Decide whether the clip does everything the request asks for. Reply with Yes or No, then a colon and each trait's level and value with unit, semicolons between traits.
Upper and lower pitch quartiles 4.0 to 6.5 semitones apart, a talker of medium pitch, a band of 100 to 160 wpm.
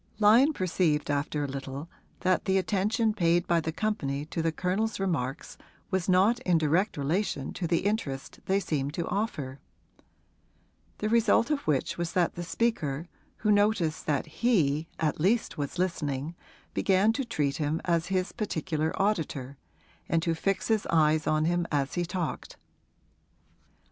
Yes: average, 4.8 semitones; medium, 170 Hz; average, 155 wpm